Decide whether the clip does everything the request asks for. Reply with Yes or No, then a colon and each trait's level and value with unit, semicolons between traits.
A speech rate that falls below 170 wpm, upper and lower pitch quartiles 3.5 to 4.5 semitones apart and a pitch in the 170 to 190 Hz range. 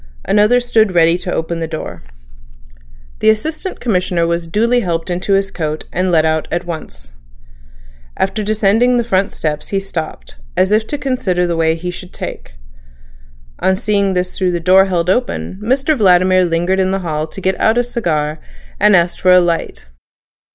No: average, 180 wpm; average, 3.9 semitones; medium, 185 Hz